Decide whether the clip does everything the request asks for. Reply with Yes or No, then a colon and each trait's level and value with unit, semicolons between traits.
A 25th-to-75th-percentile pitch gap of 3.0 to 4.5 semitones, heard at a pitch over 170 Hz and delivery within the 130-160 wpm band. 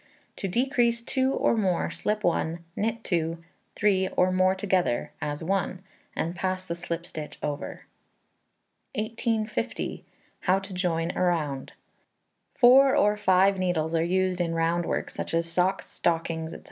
Yes: average, 3.8 semitones; medium, 185 Hz; average, 145 wpm